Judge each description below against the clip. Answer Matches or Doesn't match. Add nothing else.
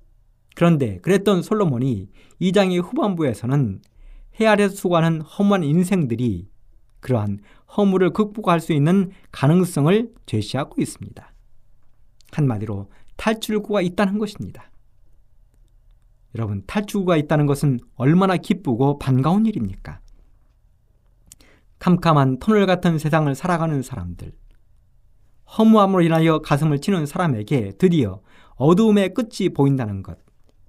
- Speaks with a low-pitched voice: Doesn't match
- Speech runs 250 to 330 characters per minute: Matches